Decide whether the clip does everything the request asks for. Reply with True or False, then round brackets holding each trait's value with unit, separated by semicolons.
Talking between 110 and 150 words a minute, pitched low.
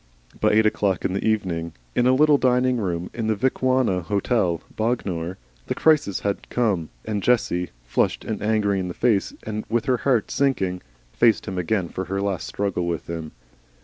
False (180 wpm; 100 Hz)